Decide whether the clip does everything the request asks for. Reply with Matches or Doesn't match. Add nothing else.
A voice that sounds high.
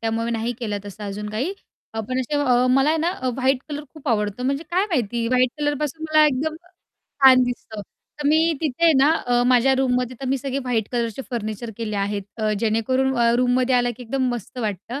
Matches